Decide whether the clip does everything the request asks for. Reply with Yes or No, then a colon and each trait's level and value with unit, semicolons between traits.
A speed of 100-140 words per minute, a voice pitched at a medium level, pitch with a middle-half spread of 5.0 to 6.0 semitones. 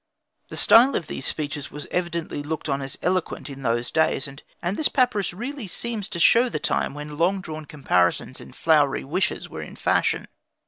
No: average, 185 wpm; medium, 160 Hz; average, 5.3 semitones